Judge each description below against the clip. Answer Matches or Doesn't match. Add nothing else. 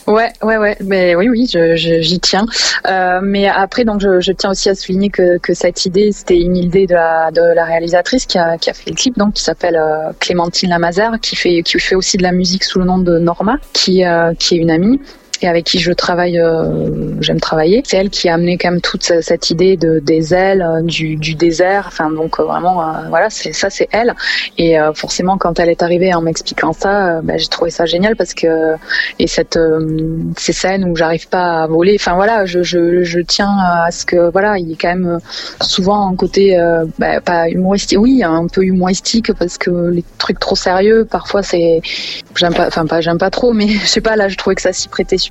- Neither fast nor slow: Doesn't match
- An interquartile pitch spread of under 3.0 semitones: Matches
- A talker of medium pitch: Matches